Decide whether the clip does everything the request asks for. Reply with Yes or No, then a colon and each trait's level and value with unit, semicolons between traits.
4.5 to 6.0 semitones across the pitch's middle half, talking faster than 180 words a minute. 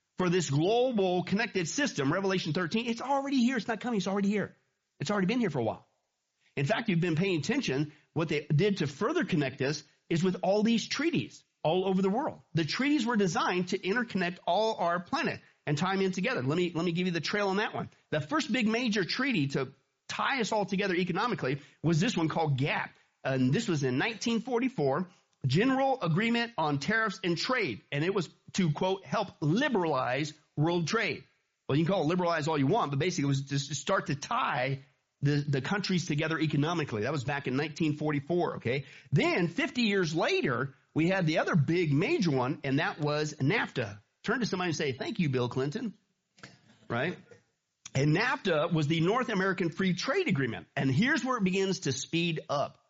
Yes: wide, 5.5 semitones; average, 200 wpm